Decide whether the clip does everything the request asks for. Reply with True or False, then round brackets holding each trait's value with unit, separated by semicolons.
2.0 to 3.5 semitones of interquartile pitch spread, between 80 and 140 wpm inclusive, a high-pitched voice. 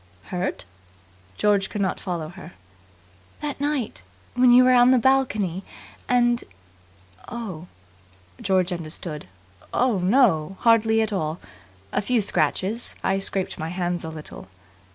False (5.6 semitones; 135 wpm; 195 Hz)